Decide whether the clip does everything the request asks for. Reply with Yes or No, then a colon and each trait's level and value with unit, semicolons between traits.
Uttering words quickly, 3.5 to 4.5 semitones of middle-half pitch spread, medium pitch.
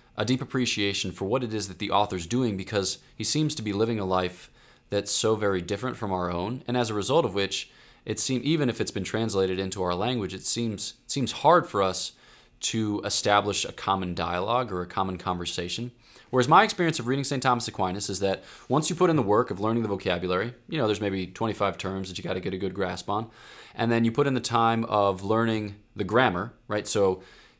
No: fast, 230 wpm; average, 3.9 semitones; low, 105 Hz